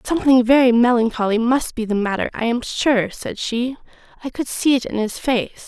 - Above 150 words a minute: Yes, average, 200 wpm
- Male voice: No, female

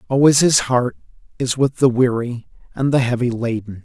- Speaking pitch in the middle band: No, low, 125 Hz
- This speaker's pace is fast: No, average, 170 wpm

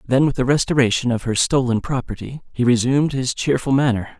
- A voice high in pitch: No, low, 130 Hz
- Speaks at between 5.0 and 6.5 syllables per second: Yes, 5.9 syllables/s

